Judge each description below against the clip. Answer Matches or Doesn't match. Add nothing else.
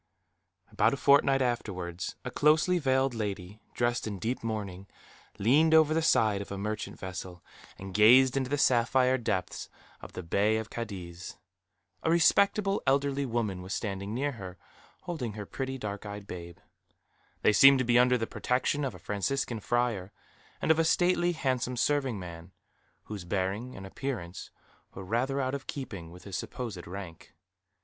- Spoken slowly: Doesn't match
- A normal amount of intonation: Doesn't match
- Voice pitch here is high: Doesn't match